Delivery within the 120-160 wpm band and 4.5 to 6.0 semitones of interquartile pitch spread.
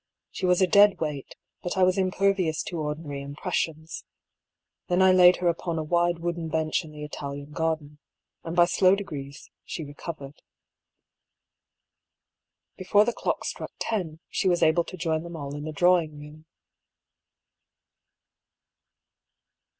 No: average, 150 wpm; average, 3.2 semitones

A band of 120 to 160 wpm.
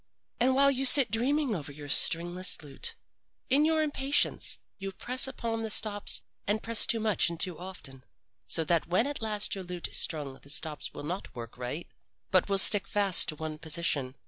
No: average, 195 wpm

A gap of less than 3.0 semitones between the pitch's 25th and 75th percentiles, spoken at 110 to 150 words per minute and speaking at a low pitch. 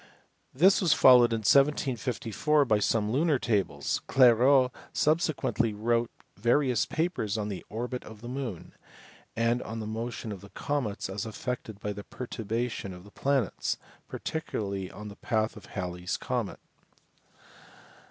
No: average, 3.7 semitones; average, 145 wpm; low, 115 Hz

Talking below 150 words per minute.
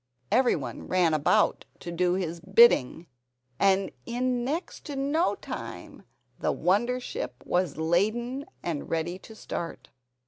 Yes: slow, 135 wpm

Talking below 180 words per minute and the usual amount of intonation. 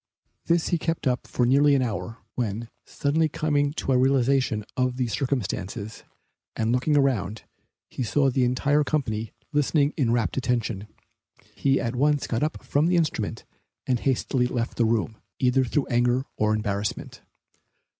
Yes: average, 155 wpm; average, 3.7 semitones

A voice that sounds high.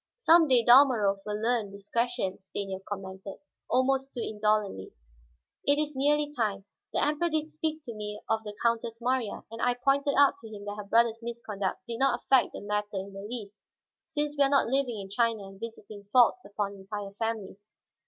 Yes: high, 225 Hz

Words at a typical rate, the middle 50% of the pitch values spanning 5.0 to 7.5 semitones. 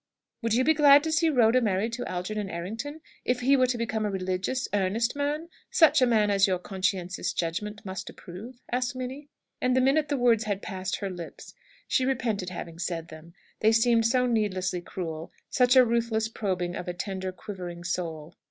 Yes: average, 190 wpm; average, 5.3 semitones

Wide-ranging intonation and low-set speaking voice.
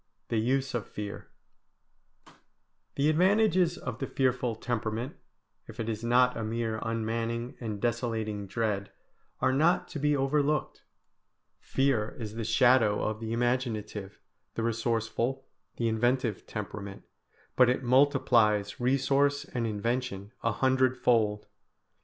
No: average, 3.0 semitones; low, 120 Hz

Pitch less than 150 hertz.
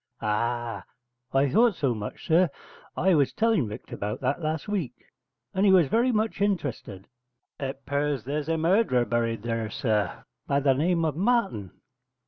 Yes: medium, 140 Hz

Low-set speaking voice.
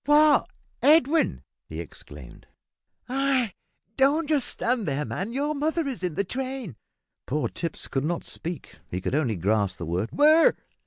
No: high, 235 Hz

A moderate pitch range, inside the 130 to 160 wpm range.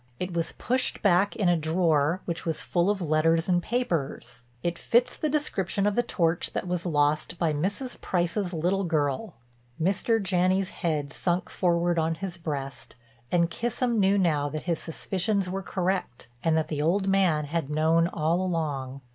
No: average, 3.4 semitones; average, 170 wpm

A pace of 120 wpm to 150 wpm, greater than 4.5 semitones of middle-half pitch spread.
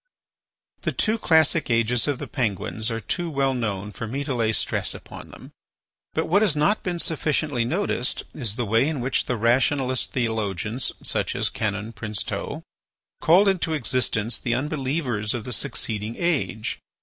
No: average, 160 wpm; average, 5.2 semitones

